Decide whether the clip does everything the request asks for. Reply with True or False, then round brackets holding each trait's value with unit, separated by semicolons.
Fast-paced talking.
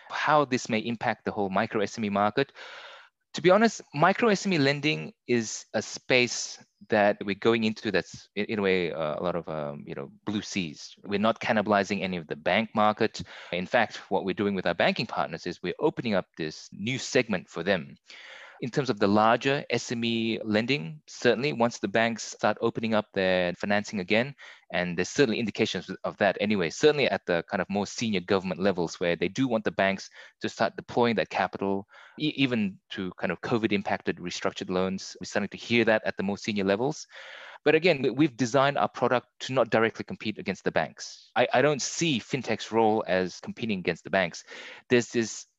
False (195 wpm)